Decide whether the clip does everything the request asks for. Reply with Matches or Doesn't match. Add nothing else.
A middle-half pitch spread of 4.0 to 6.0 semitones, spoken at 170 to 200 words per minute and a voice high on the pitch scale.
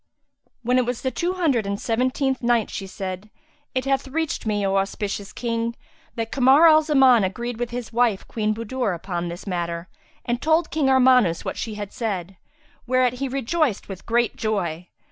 Matches